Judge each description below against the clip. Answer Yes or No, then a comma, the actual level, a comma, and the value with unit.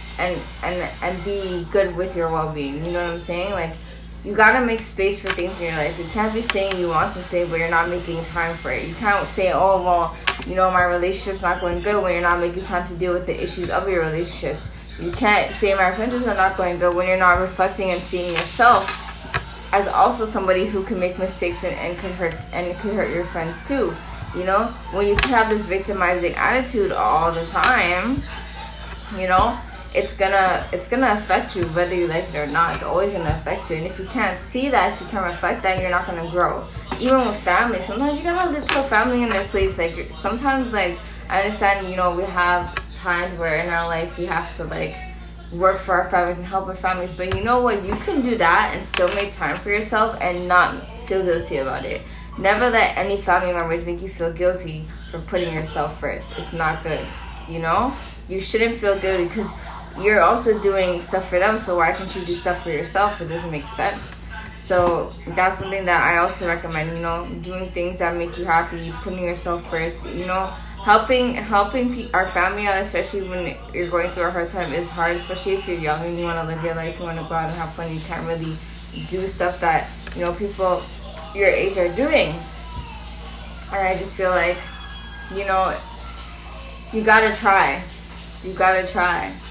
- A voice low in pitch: No, medium, 180 Hz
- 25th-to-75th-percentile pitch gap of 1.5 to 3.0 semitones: Yes, narrow, 2.5 semitones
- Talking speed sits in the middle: No, fast, 215 wpm